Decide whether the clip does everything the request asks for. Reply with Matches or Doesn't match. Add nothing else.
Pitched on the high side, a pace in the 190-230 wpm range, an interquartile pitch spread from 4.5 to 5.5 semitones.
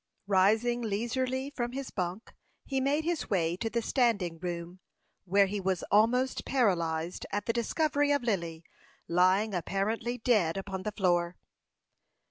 Doesn't match